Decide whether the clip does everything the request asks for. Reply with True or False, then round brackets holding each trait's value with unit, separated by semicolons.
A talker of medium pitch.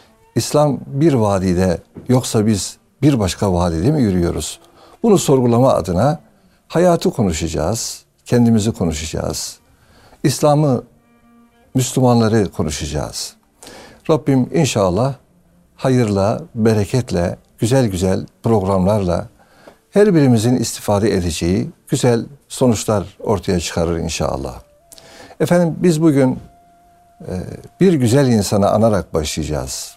False (115 Hz)